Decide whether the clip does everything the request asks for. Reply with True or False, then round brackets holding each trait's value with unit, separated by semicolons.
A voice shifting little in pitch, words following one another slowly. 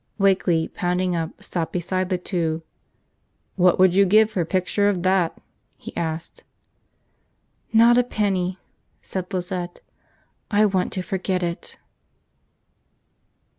True (1.9 semitones; 125 wpm)